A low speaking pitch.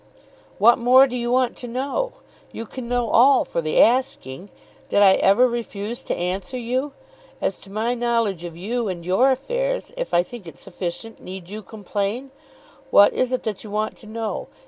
No: high, 230 Hz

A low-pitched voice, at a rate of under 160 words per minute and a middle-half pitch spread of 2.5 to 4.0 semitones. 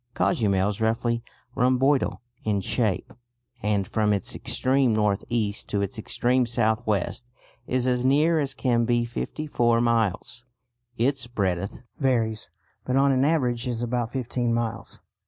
Yes: low, 120 Hz; average, 145 wpm; average, 2.8 semitones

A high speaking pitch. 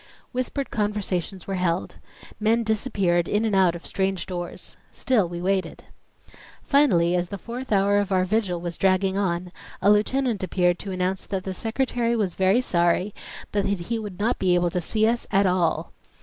Yes: high, 195 Hz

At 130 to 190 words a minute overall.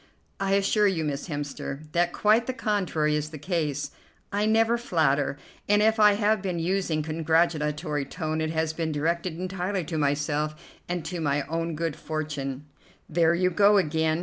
Yes: average, 175 wpm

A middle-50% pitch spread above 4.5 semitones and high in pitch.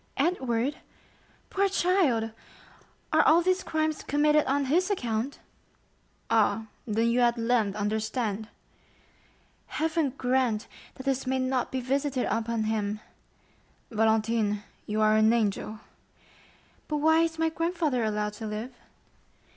Yes: wide, 5.5 semitones; high, 245 Hz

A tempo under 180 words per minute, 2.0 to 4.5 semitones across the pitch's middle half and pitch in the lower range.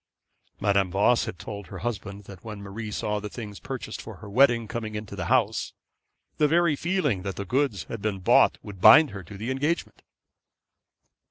No: average, 185 wpm; average, 3.8 semitones; low, 105 Hz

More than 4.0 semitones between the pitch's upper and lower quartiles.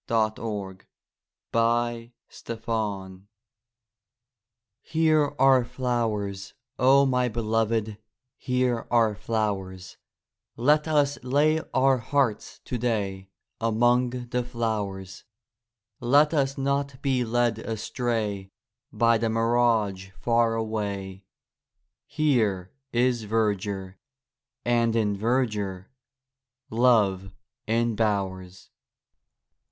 No: average, 3.3 semitones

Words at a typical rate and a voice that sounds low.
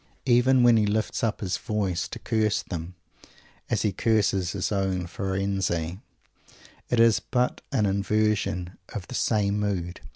Yes: average, 150 wpm; low, 100 Hz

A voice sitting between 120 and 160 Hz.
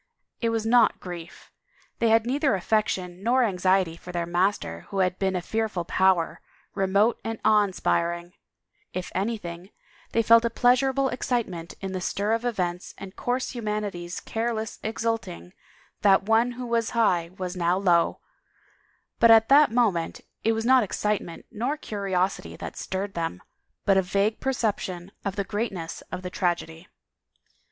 No: high, 200 Hz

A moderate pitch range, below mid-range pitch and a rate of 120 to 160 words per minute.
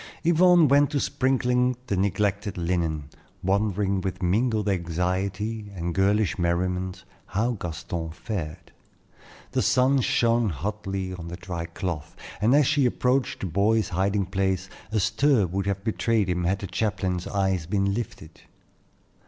Yes: average, 3.7 semitones; low, 100 Hz; average, 140 wpm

